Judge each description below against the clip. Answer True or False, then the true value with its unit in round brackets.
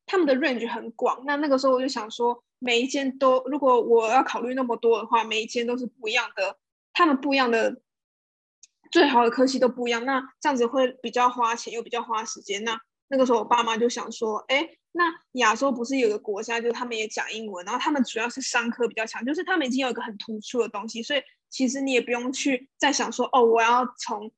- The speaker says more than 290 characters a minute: True (360 characters per minute)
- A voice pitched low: False (245 Hz)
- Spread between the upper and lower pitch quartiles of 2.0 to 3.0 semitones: True (2.4 semitones)